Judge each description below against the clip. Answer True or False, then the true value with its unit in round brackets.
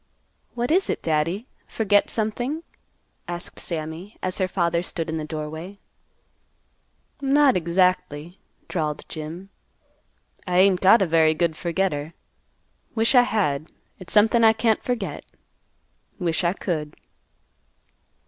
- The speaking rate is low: True (120 wpm)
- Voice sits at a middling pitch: True (180 Hz)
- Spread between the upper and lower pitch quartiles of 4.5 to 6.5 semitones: True (5.2 semitones)